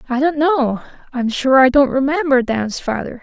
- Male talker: No, female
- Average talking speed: Yes, average, 185 wpm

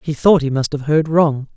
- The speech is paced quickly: Yes, fast, 270 wpm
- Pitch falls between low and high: Yes, medium, 150 Hz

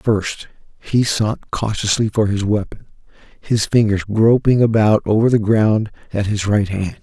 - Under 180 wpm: Yes, average, 155 wpm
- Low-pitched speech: Yes, low, 105 Hz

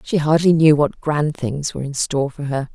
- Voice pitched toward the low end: No, medium, 145 Hz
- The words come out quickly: Yes, fast, 240 wpm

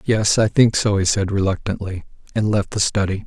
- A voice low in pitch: Yes, low, 100 Hz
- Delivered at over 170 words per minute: Yes, average, 200 wpm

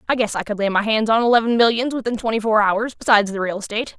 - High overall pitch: Yes, high, 220 Hz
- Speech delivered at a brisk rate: Yes, fast, 270 wpm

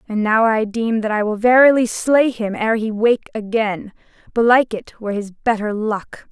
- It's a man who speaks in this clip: No, female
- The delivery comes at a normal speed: Yes, average, 190 wpm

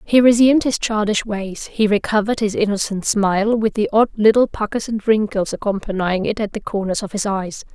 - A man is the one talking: No, female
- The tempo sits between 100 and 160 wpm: No, average, 195 wpm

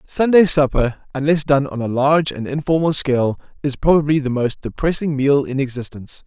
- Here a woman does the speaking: No, male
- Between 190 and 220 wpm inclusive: No, average, 170 wpm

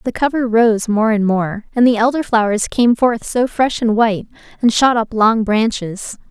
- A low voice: No, high, 225 Hz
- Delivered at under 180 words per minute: No, average, 200 wpm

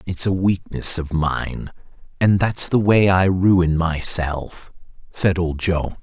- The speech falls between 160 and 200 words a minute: No, average, 150 wpm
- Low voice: Yes, very low, 90 Hz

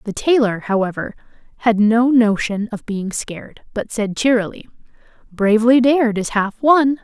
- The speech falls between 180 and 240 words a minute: No, average, 145 wpm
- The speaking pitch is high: Yes, high, 225 Hz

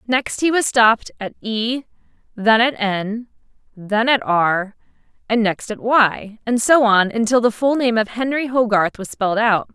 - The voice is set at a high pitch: Yes, high, 225 Hz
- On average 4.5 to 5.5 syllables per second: No, 4.2 syllables/s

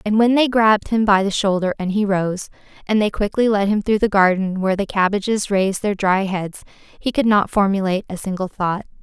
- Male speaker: No, female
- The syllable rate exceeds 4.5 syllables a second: Yes, 5.5 syllables/s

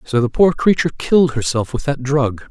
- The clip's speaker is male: Yes, male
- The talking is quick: Yes, fast, 215 wpm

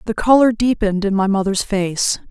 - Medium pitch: No, high, 205 Hz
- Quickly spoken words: No, average, 180 wpm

